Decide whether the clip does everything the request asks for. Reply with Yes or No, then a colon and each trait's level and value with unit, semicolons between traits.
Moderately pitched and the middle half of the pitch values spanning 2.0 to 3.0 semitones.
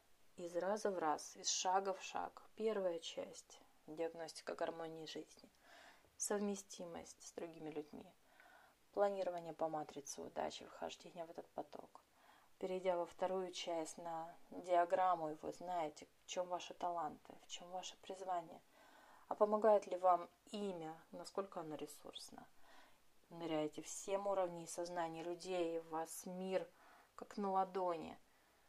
Yes: medium, 175 Hz; narrow, 2.5 semitones